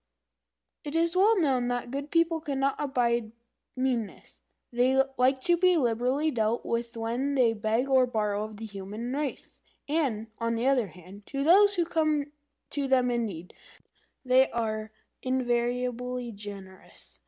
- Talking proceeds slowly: No, average, 155 wpm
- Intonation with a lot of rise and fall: No, average, 3.8 semitones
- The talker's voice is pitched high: Yes, very high, 250 Hz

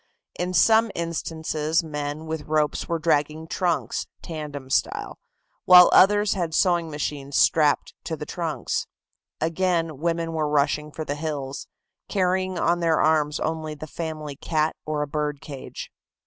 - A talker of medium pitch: Yes, medium, 160 Hz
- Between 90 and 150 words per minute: Yes, average, 145 wpm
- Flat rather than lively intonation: Yes, narrow, 2.1 semitones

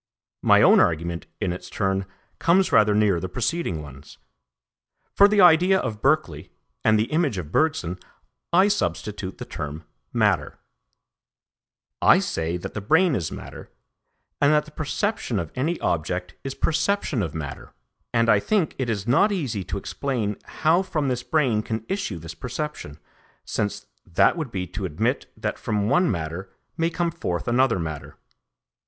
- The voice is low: Yes, low, 110 Hz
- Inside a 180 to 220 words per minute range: No, average, 160 wpm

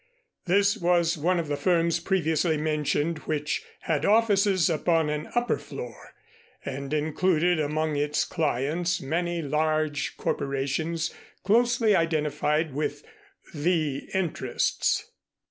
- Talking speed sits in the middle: No, slow, 110 wpm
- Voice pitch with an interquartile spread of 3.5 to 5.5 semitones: No, average, 2.8 semitones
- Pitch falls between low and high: Yes, medium, 160 Hz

